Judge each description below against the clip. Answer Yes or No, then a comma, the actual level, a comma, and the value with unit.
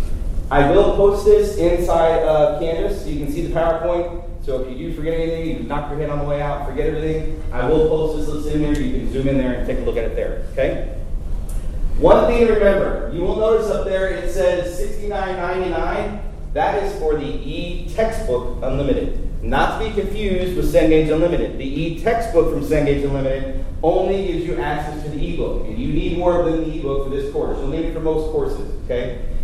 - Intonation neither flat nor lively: Yes, average, 4.2 semitones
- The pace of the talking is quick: Yes, fast, 210 wpm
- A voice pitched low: No, medium, 165 Hz